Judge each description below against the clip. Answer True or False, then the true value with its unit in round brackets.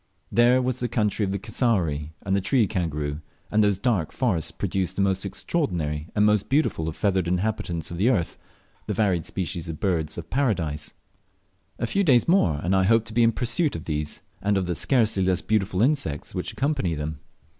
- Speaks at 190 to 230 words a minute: True (205 wpm)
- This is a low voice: True (95 Hz)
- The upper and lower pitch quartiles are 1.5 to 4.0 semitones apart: False (5.6 semitones)